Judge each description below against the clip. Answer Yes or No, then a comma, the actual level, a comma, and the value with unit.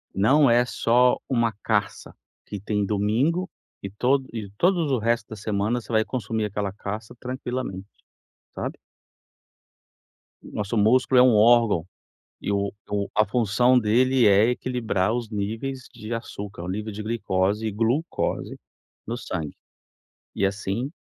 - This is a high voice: No, low, 110 Hz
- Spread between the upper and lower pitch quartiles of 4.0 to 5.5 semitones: No, average, 3.2 semitones